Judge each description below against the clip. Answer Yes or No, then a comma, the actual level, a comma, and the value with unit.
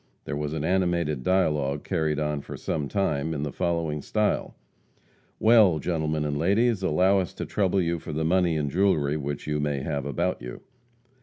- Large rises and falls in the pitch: No, average, 3.8 semitones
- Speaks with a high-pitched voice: No, very low, 80 Hz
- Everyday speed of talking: Yes, average, 180 wpm